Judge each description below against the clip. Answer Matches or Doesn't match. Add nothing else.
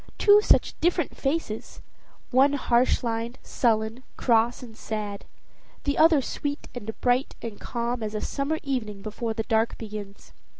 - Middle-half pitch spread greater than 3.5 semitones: Matches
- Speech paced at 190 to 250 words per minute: Doesn't match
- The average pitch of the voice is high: Matches